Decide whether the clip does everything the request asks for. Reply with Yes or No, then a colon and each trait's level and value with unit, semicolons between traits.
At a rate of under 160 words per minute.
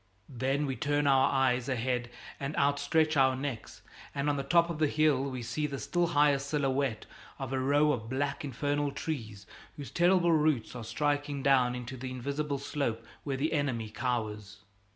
No: average, 175 wpm